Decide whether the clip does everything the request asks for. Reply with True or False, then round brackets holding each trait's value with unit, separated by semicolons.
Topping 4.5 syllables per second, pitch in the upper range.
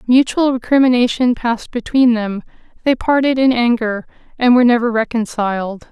True (5.4 syllables/s; 240 Hz)